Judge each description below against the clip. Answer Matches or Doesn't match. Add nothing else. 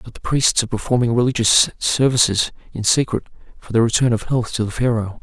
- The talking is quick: Doesn't match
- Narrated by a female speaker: Doesn't match